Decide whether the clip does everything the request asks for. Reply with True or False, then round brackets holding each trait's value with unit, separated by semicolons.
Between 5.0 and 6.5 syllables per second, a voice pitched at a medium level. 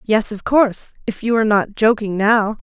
False (5.2 syllables/s; 215 Hz)